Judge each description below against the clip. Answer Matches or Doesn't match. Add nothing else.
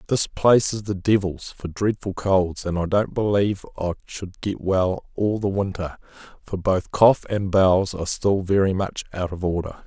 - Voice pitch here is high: Doesn't match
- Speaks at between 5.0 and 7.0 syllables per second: Doesn't match